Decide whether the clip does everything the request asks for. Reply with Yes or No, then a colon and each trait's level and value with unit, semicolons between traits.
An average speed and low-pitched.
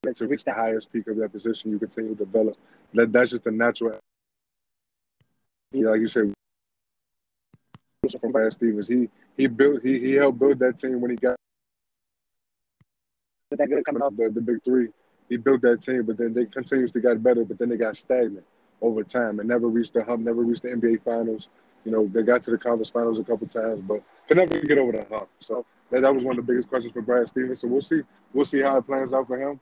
No: fast, 225 wpm; low, 120 Hz